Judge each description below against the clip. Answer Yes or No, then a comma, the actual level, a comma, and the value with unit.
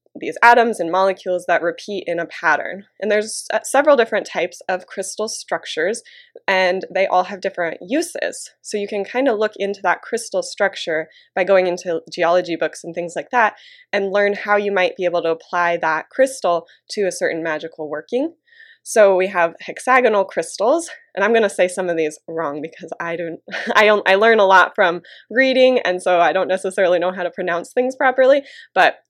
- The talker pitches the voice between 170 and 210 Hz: Yes, high, 190 Hz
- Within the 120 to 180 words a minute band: No, average, 200 wpm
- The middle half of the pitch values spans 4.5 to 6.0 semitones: Yes, average, 4.8 semitones